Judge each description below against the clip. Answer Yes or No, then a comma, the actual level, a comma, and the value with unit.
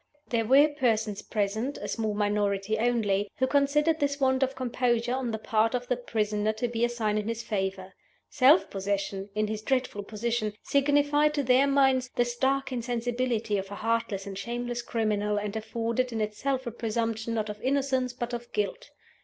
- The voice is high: Yes, high, 235 Hz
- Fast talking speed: No, average, 180 wpm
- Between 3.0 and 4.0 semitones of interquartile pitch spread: Yes, average, 3.4 semitones